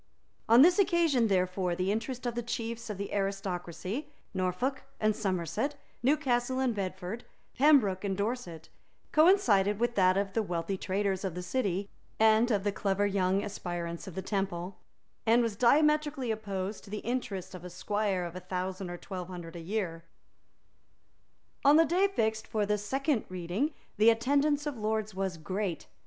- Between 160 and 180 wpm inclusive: Yes, average, 165 wpm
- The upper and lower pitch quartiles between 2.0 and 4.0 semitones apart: No, average, 4.6 semitones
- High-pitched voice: Yes, high, 205 Hz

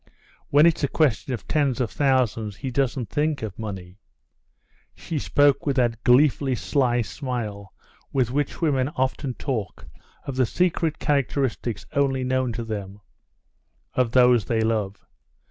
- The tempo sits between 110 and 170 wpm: Yes, average, 140 wpm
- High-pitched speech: No, low, 130 Hz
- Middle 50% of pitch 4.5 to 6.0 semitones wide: No, average, 3.9 semitones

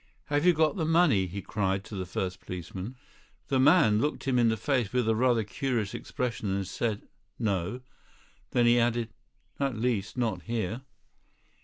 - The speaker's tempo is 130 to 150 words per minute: No, average, 170 wpm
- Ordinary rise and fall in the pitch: Yes, average, 4.6 semitones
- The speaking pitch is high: No, low, 115 Hz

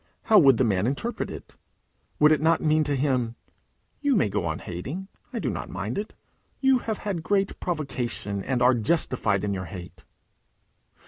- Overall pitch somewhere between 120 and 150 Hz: Yes, low, 135 Hz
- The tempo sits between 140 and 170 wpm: No, average, 180 wpm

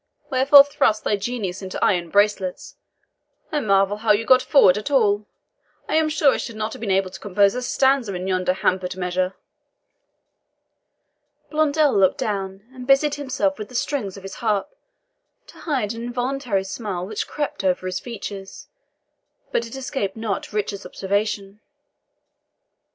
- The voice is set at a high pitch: Yes, high, 210 Hz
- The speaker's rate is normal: Yes, average, 155 wpm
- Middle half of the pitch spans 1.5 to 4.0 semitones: No, average, 4.9 semitones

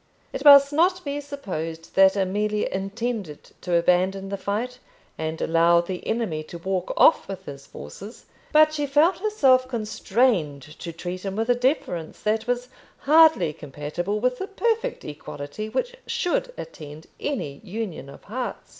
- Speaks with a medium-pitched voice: No, high, 210 Hz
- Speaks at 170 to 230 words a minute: No, average, 155 wpm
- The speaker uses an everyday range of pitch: No, wide, 7.6 semitones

